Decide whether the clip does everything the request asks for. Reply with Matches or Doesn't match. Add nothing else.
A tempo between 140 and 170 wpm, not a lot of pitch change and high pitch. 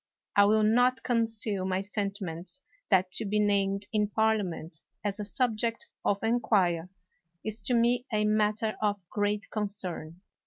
Matches